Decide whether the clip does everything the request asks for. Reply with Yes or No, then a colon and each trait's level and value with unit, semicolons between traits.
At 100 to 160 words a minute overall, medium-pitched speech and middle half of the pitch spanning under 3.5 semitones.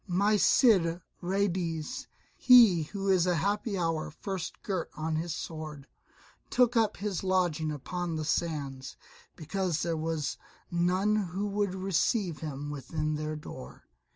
No: slow, 135 wpm; medium, 175 Hz; average, 3.9 semitones